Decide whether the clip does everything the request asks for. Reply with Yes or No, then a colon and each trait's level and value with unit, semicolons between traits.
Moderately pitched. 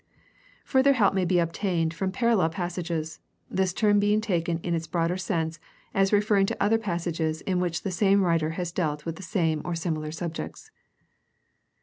Yes: medium, 175 Hz